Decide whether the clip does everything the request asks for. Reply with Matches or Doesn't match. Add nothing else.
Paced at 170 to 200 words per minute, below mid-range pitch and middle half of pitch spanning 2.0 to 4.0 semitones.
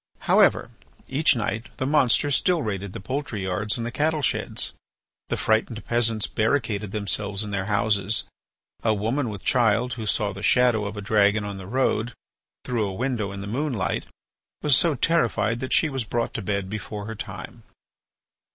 Matches